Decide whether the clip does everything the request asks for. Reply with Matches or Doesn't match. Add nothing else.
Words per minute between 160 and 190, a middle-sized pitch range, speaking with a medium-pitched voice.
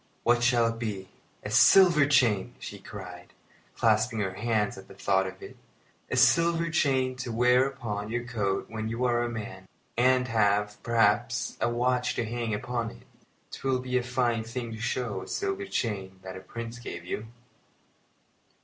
Doesn't match